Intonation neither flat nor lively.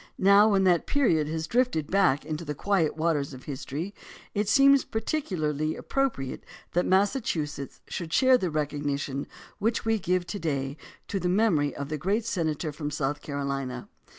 No: wide, 5.7 semitones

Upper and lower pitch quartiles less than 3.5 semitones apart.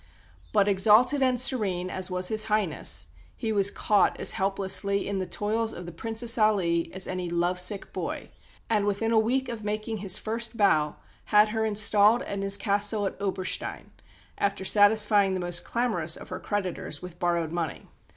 Yes: average, 3.0 semitones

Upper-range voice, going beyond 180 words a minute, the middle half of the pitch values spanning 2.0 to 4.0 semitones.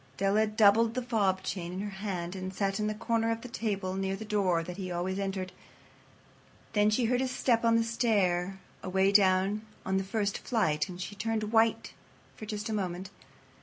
Yes: high, 200 Hz; average, 200 wpm; average, 2.8 semitones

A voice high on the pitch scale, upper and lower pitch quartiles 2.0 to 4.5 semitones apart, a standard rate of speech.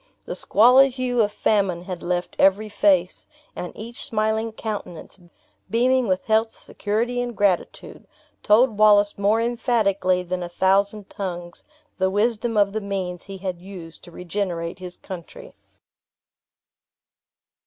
No: high, 200 Hz; average, 3.3 semitones; slow, 130 wpm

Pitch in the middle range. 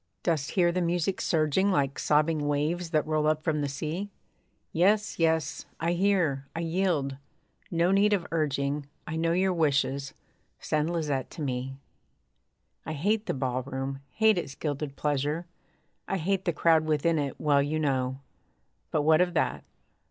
Yes: medium, 155 Hz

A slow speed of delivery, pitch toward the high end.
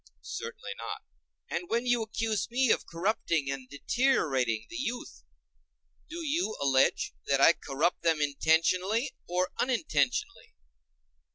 No: slow, 115 wpm; medium, 180 Hz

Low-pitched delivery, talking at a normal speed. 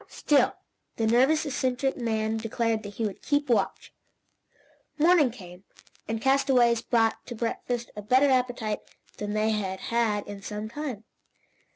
No: high, 235 Hz; average, 145 wpm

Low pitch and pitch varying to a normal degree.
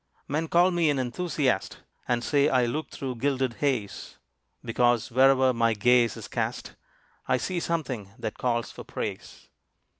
Yes: low, 130 Hz; average, 3.5 semitones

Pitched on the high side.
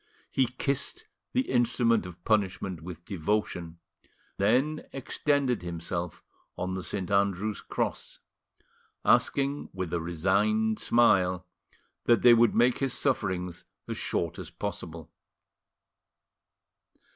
No: low, 100 Hz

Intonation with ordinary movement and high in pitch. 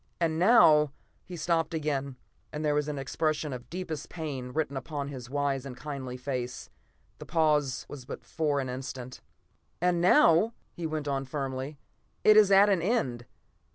No: average, 3.5 semitones; medium, 150 Hz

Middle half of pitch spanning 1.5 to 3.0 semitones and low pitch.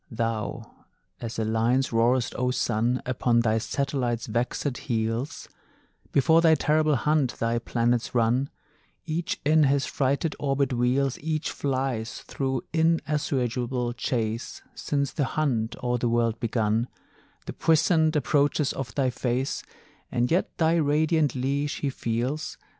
No: average, 3.7 semitones; low, 130 Hz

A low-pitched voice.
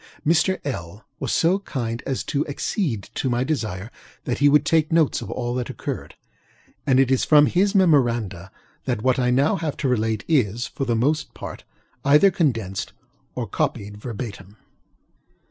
Yes: low, 130 Hz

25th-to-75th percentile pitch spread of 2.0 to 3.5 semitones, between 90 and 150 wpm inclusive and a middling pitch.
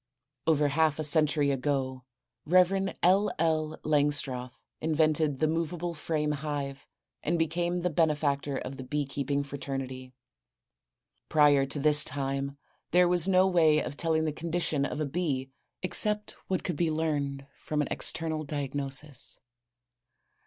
Yes: narrow, 2.6 semitones; average, 140 wpm; medium, 150 Hz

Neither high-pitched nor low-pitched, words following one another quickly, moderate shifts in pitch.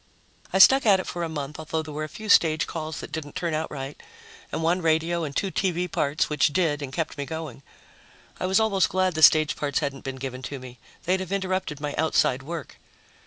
Yes: medium, 160 Hz; fast, 225 wpm; average, 3.7 semitones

